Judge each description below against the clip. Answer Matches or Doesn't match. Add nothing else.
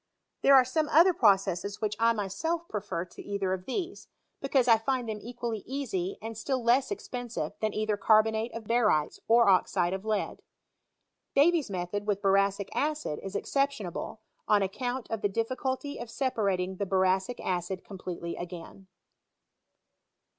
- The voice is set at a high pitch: Matches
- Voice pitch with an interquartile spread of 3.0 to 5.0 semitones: Matches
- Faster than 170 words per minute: Doesn't match